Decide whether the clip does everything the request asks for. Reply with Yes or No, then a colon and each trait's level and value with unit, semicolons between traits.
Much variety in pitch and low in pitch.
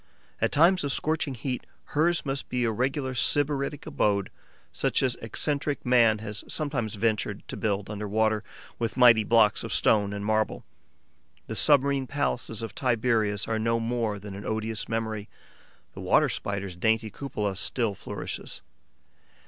No: average, 4.0 semitones; low, 115 Hz